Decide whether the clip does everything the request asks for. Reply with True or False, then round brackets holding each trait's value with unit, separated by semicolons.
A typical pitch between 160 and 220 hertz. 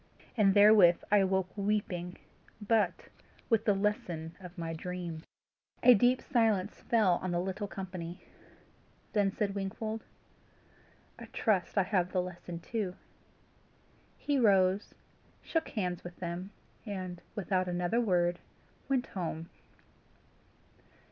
True (190 Hz)